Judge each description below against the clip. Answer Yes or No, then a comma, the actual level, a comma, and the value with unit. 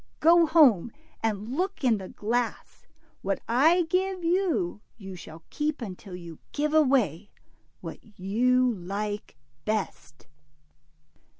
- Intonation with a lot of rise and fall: Yes, wide, 7.9 semitones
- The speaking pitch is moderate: No, high, 235 Hz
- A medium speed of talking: No, slow, 115 wpm